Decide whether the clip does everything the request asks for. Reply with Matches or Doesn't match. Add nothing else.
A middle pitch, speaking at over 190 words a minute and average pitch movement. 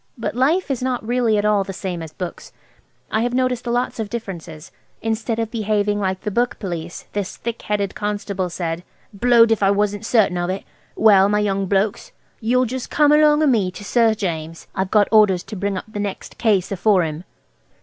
Doesn't match